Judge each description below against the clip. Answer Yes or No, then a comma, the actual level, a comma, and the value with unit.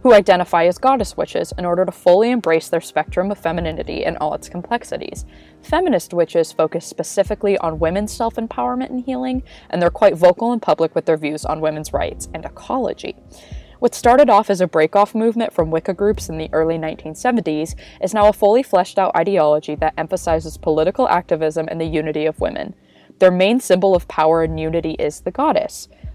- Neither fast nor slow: Yes, average, 185 wpm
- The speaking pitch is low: No, medium, 175 Hz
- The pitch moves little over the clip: No, average, 4.7 semitones